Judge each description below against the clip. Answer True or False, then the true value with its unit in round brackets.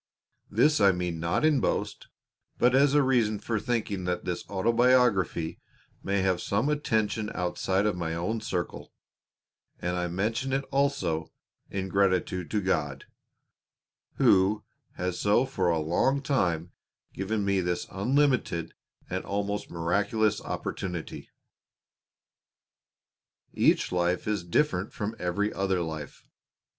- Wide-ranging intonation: False (4.3 semitones)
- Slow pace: True (125 wpm)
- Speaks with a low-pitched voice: True (100 Hz)